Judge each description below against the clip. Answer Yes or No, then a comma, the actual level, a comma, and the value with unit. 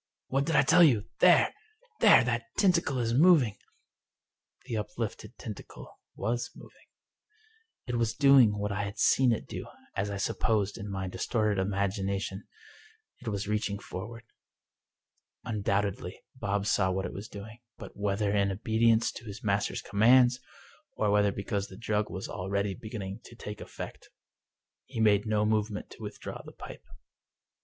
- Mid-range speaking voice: No, low, 105 Hz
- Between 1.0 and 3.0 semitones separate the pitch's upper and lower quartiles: Yes, narrow, 2.5 semitones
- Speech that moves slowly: No, average, 160 wpm